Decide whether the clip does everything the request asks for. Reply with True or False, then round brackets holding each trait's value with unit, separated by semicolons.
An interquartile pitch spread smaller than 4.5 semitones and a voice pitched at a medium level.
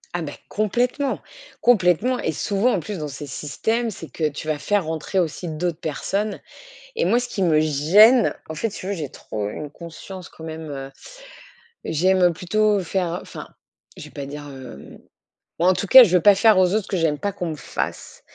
False (5.0 semitones; 175 Hz)